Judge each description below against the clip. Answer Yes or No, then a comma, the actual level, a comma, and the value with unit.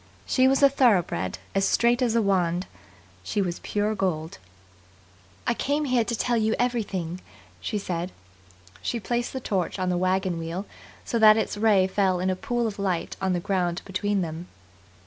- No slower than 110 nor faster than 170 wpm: No, average, 180 wpm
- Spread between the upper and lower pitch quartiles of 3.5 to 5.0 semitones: Yes, average, 4.4 semitones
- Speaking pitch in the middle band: No, high, 195 Hz